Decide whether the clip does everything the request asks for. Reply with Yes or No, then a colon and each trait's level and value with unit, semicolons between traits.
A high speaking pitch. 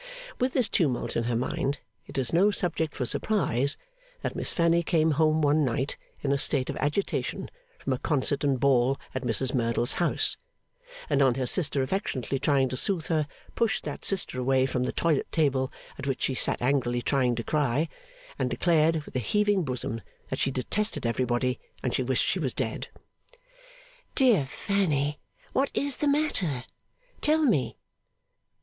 No: medium, 140 Hz